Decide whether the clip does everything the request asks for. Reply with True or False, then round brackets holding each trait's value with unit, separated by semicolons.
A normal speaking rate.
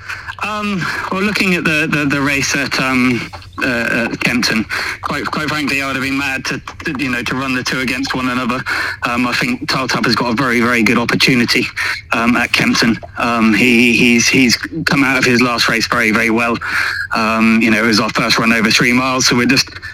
False (215 wpm)